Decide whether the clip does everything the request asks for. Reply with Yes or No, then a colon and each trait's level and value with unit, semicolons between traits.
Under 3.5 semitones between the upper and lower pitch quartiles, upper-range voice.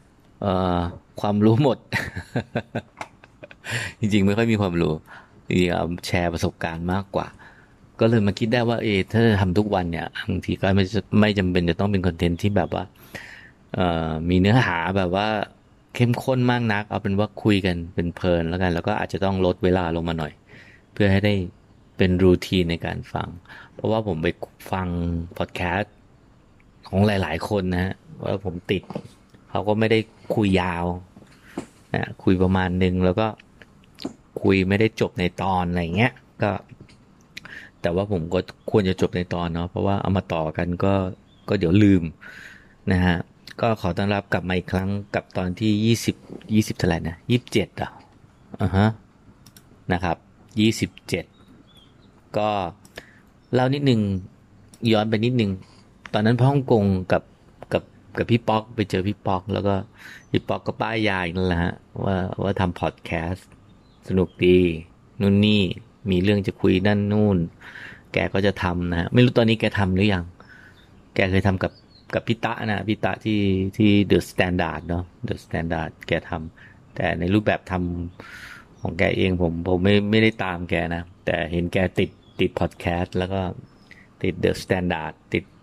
No: average, 3.0 semitones; very low, 95 Hz